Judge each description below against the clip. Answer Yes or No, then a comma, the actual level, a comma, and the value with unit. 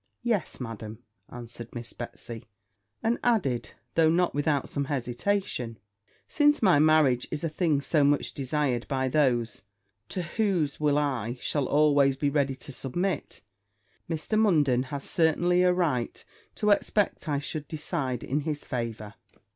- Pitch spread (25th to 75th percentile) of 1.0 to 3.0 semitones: No, average, 4.7 semitones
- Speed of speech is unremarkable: Yes, average, 145 wpm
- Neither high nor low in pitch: Yes, medium, 145 Hz